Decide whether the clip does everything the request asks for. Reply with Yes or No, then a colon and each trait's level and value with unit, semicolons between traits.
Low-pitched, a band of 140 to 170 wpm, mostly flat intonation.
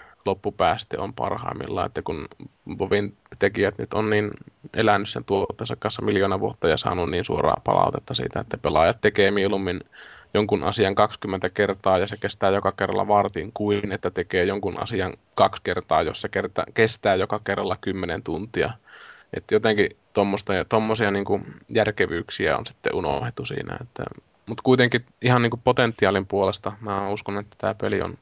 Yes: low, 100 Hz; average, 150 wpm; narrow, 2.2 semitones